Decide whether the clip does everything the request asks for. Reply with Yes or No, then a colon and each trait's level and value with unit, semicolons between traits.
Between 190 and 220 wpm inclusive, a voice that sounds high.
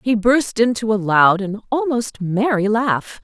No: average, 165 wpm; high, 220 Hz